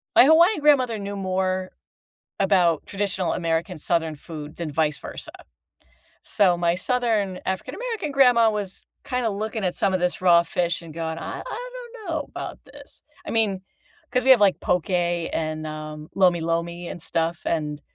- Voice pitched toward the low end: No, medium, 185 Hz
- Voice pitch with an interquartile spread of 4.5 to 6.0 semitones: Yes, average, 5.1 semitones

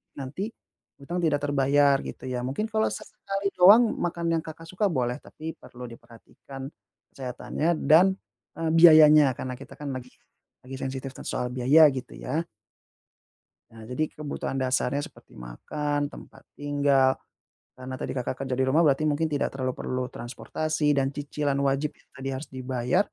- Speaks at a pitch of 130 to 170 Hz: Yes, medium, 140 Hz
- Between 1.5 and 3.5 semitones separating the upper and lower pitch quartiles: Yes, average, 3.2 semitones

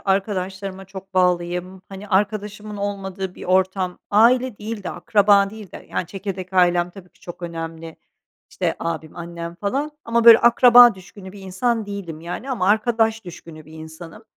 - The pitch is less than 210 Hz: Yes, high, 190 Hz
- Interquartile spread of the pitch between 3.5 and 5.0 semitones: No, average, 3.0 semitones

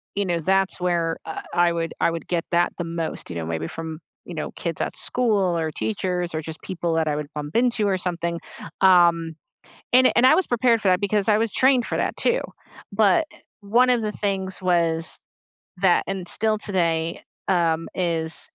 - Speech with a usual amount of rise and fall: Yes, average, 3.6 semitones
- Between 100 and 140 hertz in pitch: No, medium, 175 Hz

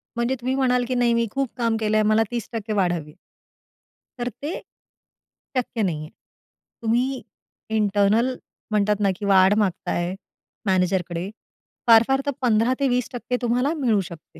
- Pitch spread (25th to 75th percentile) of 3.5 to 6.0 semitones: Yes, average, 4.0 semitones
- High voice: Yes, high, 225 Hz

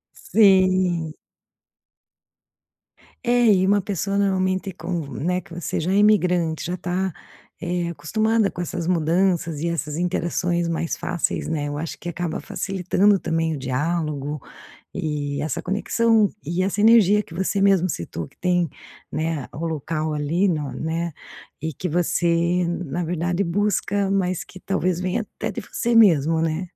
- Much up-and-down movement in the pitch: No, average, 2.9 semitones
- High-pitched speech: No, medium, 175 Hz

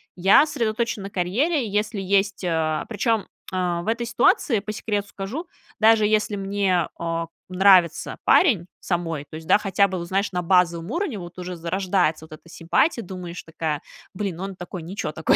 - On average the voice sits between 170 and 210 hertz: Yes, high, 190 Hz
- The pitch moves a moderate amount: Yes, average, 3.6 semitones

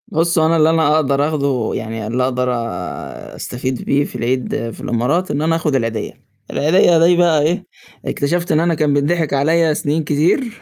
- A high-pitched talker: No, medium, 150 Hz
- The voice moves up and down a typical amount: Yes, average, 4.0 semitones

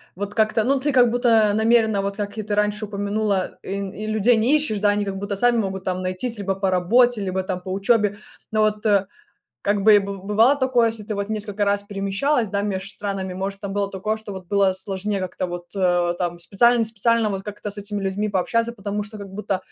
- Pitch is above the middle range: Yes, high, 205 Hz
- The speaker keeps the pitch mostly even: Yes, narrow, 2.1 semitones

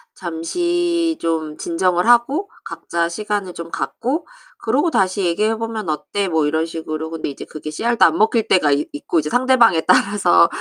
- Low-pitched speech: No, medium, 185 Hz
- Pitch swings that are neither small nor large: No, wide, 6.5 semitones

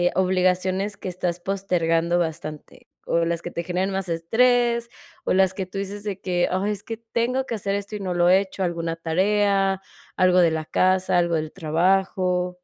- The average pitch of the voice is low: No, medium, 185 Hz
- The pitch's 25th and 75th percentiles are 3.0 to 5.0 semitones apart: No, narrow, 2.4 semitones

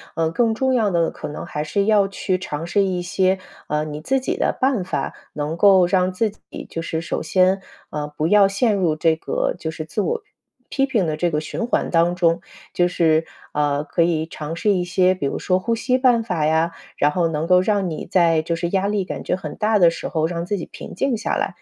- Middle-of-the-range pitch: Yes, medium, 180 Hz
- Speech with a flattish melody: No, average, 3.8 semitones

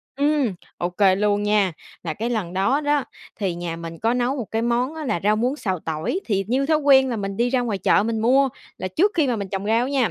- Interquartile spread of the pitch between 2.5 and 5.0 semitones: No, wide, 5.4 semitones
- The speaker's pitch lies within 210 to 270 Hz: Yes, high, 225 Hz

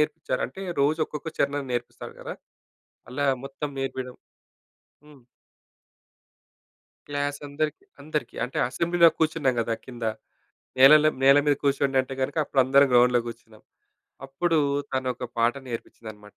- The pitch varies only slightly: No, average, 3.0 semitones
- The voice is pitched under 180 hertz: Yes, low, 135 Hz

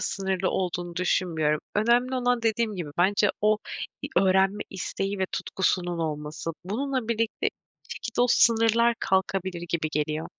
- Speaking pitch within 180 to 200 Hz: Yes, high, 190 Hz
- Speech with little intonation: No, average, 4.4 semitones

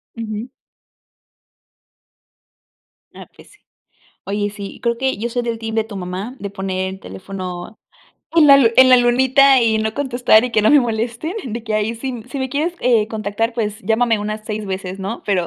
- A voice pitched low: No, high, 225 Hz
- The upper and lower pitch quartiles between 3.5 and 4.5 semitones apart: No, average, 3.1 semitones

